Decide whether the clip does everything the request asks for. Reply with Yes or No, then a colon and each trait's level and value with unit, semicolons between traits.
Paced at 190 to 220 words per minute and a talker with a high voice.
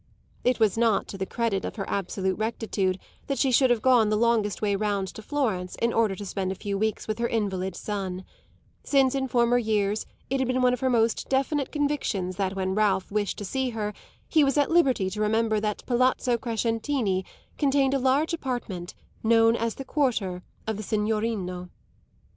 Yes: average, 195 wpm; high, 220 Hz